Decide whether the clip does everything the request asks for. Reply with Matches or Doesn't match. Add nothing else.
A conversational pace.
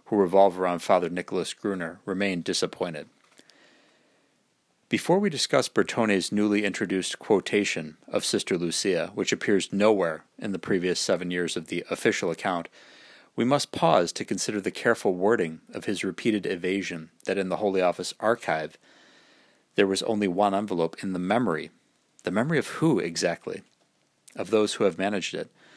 Matches